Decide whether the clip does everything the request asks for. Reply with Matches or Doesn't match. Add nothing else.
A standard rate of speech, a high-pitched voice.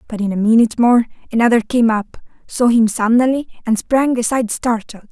Matches